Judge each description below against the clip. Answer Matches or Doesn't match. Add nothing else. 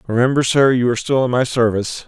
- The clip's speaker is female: Doesn't match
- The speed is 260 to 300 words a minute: Doesn't match